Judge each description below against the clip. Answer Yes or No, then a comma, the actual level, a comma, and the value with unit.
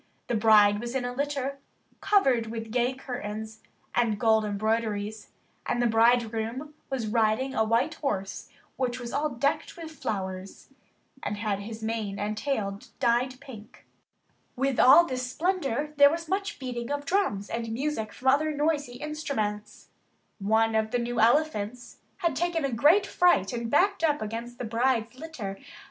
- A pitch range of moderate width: Yes, average, 4.5 semitones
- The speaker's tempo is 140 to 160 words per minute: Yes, average, 155 wpm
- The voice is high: Yes, high, 240 Hz